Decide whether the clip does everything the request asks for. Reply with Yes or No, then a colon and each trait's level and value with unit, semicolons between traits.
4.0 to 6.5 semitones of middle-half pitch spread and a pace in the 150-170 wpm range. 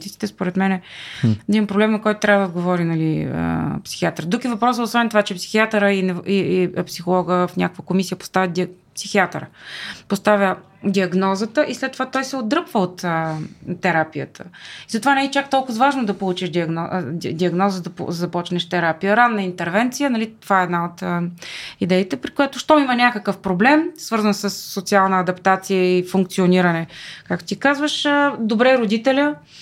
Yes: average, 4.4 semitones; fast, 165 wpm